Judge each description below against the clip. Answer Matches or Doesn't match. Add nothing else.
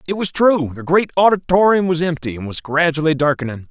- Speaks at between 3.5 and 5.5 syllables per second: Doesn't match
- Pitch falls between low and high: Matches